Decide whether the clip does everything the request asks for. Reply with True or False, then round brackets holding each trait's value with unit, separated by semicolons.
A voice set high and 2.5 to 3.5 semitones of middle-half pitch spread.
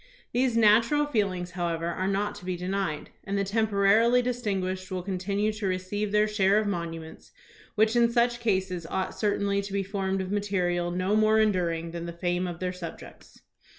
True (195 Hz; 2.8 semitones)